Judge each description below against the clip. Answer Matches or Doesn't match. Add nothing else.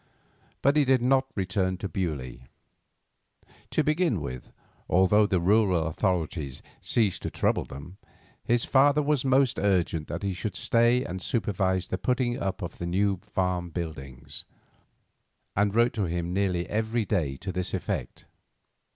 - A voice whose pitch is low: Matches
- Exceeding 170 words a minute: Doesn't match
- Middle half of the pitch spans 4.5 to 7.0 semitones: Matches